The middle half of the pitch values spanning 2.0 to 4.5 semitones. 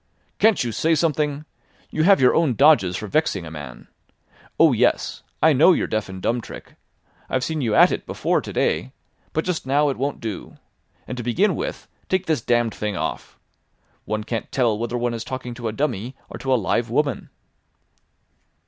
No: average, 5.3 semitones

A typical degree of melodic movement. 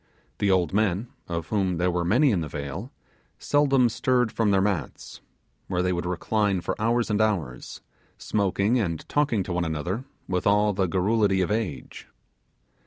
Yes: average, 3.8 semitones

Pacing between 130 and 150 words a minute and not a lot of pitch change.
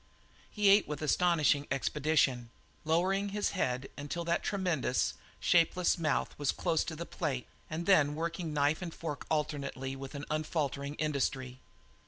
No: average, 145 wpm; average, 3.4 semitones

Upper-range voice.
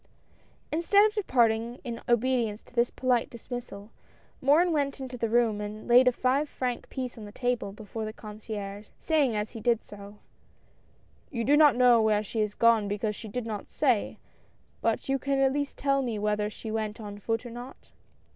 Yes: high, 235 Hz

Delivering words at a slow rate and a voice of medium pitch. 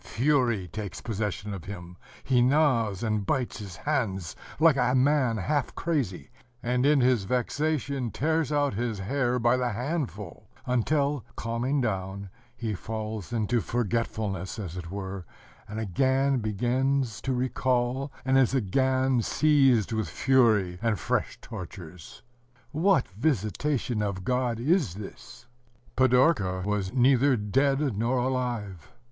No: slow, 130 wpm; low, 120 Hz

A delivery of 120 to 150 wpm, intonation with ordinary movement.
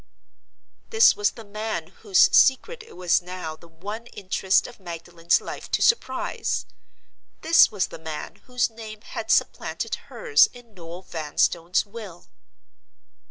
Yes: slow, 135 wpm; average, 5.0 semitones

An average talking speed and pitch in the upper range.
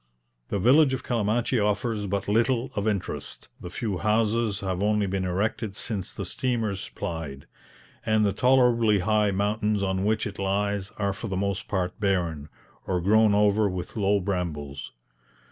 No: average, 160 wpm; low, 100 Hz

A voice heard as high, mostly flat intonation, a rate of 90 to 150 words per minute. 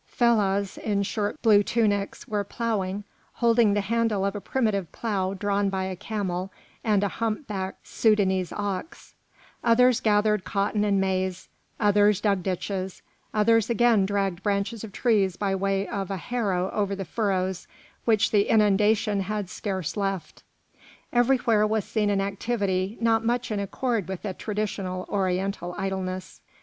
Yes: high, 200 Hz; narrow, 2.2 semitones; average, 145 wpm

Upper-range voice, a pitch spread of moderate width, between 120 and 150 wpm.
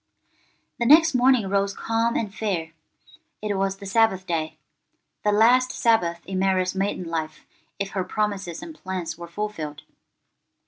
Yes: high, 195 Hz; average, 3.6 semitones; average, 145 wpm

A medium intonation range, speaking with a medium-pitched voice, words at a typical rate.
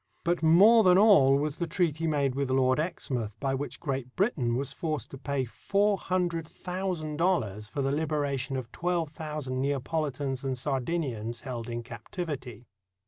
Yes: average, 4.4 semitones; medium, 145 Hz; average, 160 wpm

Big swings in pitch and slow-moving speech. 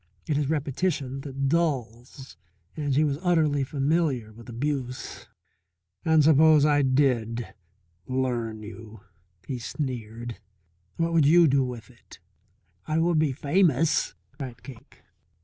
No: average, 3.9 semitones; slow, 125 wpm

